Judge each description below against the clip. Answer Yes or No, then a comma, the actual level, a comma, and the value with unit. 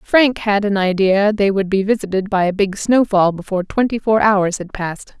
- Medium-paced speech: No, fast, 210 wpm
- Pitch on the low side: No, high, 200 Hz